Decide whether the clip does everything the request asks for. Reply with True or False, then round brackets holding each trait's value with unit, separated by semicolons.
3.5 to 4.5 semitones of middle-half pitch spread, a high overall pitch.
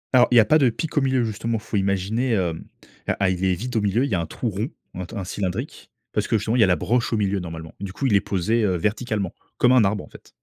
False (4.1 semitones; 105 Hz)